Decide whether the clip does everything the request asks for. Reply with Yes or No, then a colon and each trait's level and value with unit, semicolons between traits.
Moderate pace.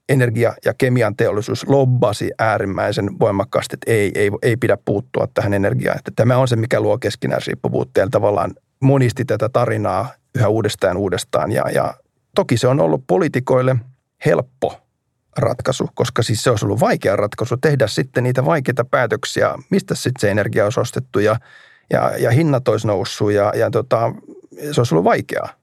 No: fast, 165 wpm